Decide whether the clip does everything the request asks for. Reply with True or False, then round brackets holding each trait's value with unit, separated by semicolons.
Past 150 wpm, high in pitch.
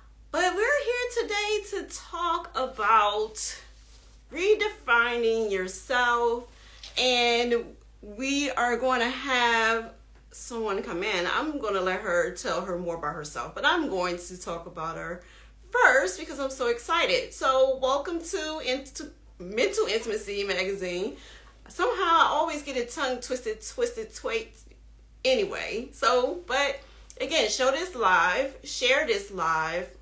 False (135 wpm; 260 Hz)